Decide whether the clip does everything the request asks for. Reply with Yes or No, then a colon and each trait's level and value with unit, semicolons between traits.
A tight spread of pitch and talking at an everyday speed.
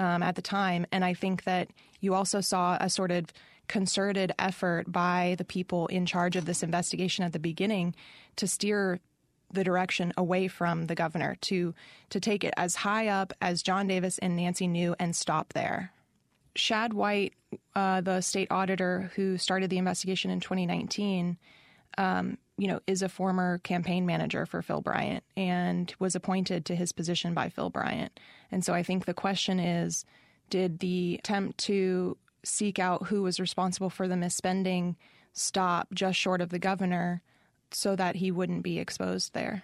Yes: narrow, 1.3 semitones; average, 175 wpm